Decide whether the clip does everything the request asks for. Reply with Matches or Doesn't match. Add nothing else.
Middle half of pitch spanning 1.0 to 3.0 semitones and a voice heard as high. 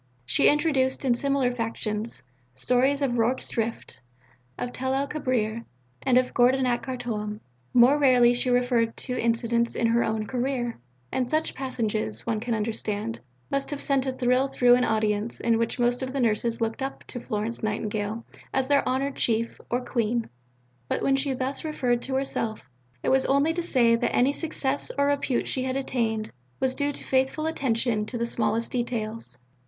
Matches